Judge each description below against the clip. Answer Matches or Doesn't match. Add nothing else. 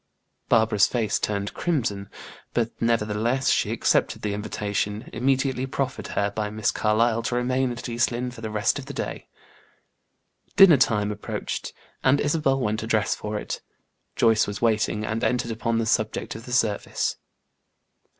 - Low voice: Matches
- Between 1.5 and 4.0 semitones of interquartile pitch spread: Matches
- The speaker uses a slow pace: Doesn't match